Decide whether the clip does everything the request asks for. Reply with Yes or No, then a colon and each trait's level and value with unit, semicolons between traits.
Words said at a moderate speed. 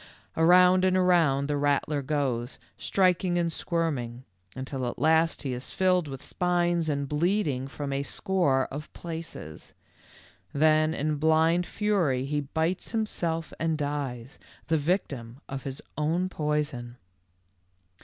No: slow, 130 wpm